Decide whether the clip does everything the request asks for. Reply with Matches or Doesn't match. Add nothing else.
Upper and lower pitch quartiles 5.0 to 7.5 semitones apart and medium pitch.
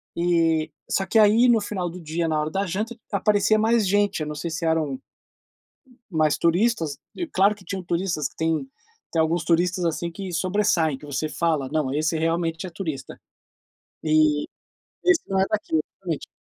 Doesn't match